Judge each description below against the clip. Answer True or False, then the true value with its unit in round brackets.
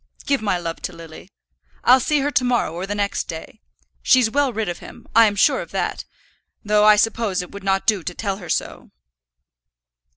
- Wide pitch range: False (4.0 semitones)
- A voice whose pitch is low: False (205 Hz)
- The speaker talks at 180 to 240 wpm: True (200 wpm)